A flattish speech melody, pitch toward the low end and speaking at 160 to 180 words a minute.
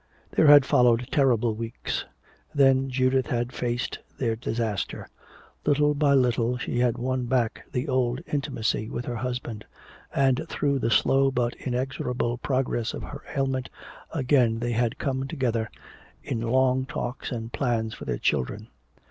No: narrow, 2.2 semitones; low, 125 Hz; average, 150 wpm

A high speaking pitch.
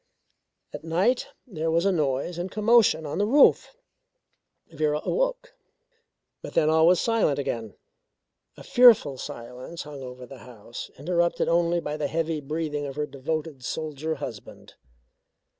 No: medium, 160 Hz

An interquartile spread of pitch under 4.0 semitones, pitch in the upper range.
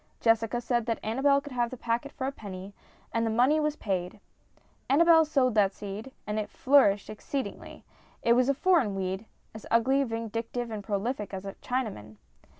No: average, 4.3 semitones; high, 230 Hz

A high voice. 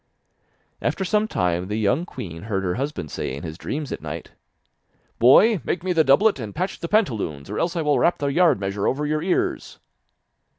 No: low, 135 Hz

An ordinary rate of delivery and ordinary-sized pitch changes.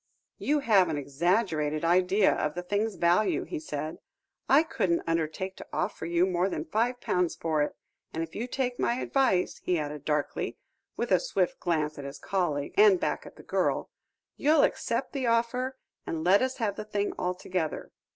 No: average, 180 wpm; wide, 6.5 semitones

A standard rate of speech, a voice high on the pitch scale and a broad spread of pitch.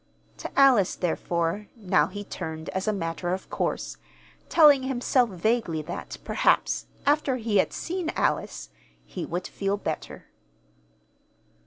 No: slow, 130 wpm; high, 205 Hz; wide, 6.4 semitones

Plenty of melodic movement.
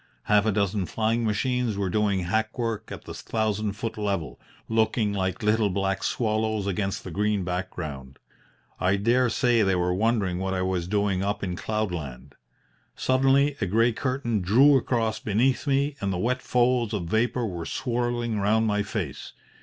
No: average, 3.5 semitones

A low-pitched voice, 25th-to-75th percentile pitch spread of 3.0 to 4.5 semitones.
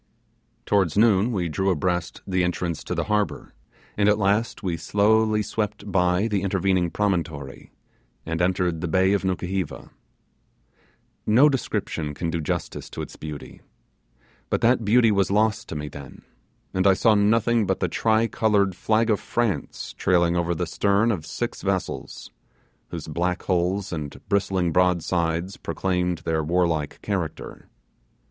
Yes: very low, 95 Hz; average, 3.4 semitones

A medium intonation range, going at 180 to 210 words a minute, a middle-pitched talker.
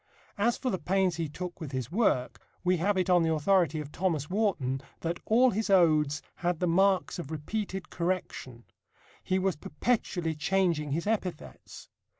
No: average, 3.9 semitones; average, 165 wpm; medium, 175 Hz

